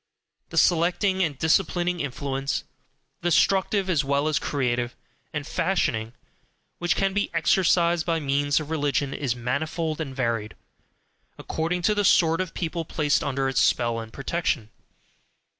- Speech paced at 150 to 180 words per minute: No, average, 140 wpm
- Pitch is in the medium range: Yes, medium, 155 Hz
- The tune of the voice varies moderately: Yes, average, 4.2 semitones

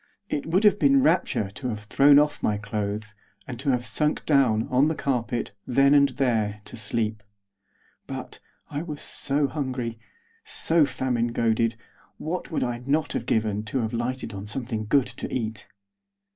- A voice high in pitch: No, low, 125 Hz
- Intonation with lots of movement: No, average, 4.5 semitones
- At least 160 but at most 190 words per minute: Yes, average, 170 wpm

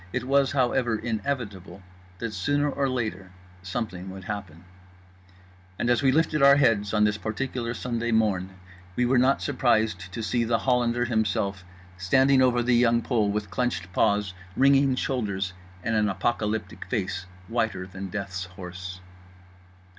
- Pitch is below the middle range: Yes, low, 110 Hz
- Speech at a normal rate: Yes, average, 145 wpm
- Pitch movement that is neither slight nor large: Yes, average, 4.7 semitones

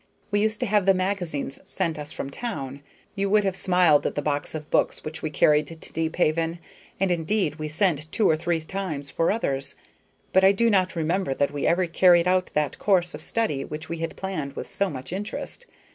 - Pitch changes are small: No, average, 4.1 semitones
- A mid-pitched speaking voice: Yes, medium, 170 Hz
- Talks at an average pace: No, fast, 210 wpm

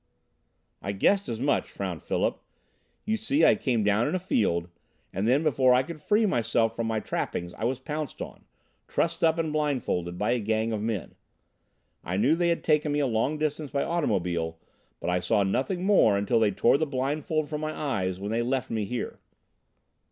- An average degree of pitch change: No, wide, 6.8 semitones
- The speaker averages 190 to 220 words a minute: Yes, average, 195 wpm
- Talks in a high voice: No, low, 125 Hz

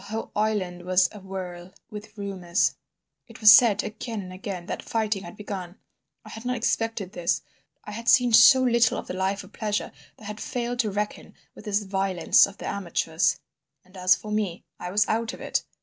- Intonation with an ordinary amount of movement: Yes, average, 3.0 semitones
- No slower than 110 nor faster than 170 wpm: No, average, 200 wpm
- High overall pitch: Yes, high, 205 Hz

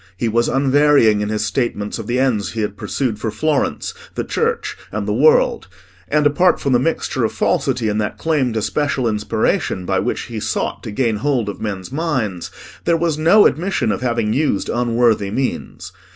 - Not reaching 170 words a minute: No, average, 190 wpm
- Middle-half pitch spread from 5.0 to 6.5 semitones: Yes, wide, 5.6 semitones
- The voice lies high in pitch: No, low, 120 Hz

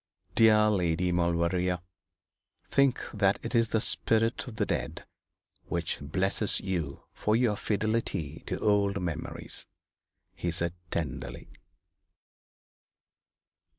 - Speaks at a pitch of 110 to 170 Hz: No, very low, 95 Hz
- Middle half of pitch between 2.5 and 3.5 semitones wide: No, average, 4.2 semitones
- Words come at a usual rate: No, slow, 105 wpm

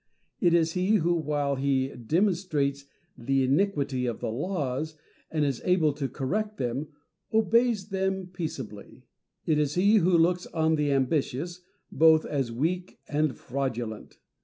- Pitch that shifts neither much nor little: Yes, average, 5.0 semitones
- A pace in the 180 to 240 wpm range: No, average, 140 wpm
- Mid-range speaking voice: Yes, medium, 155 Hz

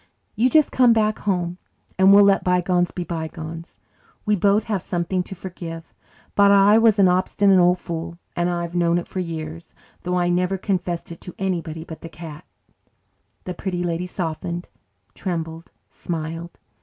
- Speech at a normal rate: Yes, average, 165 wpm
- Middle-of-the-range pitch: Yes, medium, 175 Hz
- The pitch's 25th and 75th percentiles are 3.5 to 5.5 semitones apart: No, narrow, 2.4 semitones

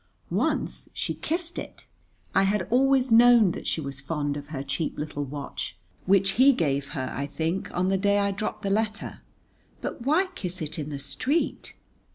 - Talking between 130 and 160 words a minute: No, average, 185 wpm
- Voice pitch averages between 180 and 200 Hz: Yes, high, 190 Hz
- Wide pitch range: Yes, wide, 7.7 semitones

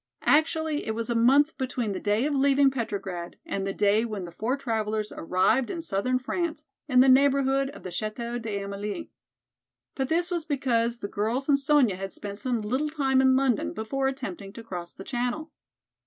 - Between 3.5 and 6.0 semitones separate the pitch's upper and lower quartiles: Yes, average, 4.7 semitones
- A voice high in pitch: Yes, high, 245 Hz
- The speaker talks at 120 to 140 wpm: No, average, 185 wpm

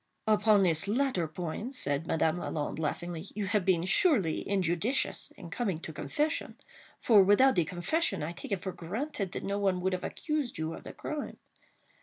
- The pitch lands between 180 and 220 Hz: Yes, high, 190 Hz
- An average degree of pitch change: Yes, average, 5.0 semitones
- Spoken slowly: No, average, 180 wpm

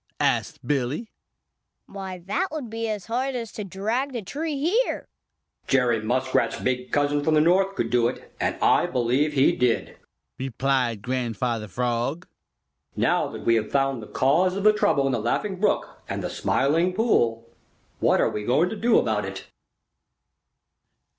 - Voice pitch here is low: No, medium, 145 Hz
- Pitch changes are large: Yes, wide, 9.0 semitones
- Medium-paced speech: Yes, average, 165 wpm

